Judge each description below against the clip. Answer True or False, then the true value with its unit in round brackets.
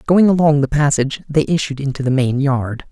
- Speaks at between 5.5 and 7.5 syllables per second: True (5.6 syllables/s)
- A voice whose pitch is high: False (140 Hz)